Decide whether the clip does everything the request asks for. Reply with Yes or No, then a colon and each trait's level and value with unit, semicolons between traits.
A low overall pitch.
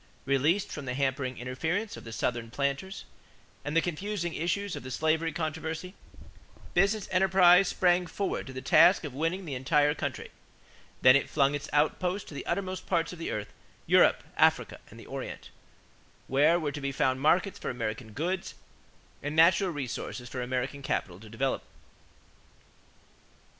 No: medium, 150 Hz